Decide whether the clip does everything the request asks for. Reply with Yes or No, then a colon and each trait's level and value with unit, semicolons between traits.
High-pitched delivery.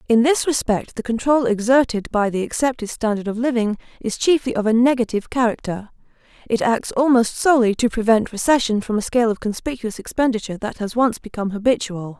Yes: high, 230 Hz